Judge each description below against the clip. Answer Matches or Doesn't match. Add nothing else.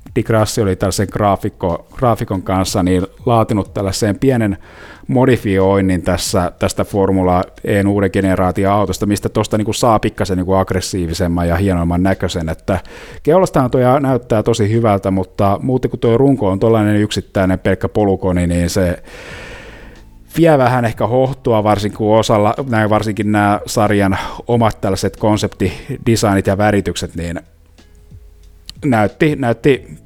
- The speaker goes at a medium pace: Matches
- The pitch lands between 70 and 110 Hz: Matches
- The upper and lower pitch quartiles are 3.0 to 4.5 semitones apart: Matches